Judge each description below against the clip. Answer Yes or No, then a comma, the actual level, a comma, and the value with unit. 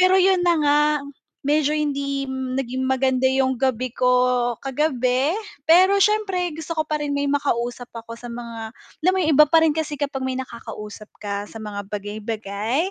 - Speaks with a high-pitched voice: Yes, very high, 265 Hz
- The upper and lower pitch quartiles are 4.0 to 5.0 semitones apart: Yes, average, 4.3 semitones